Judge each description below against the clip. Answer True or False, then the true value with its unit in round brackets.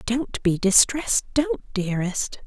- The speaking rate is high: False (120 wpm)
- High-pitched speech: True (230 Hz)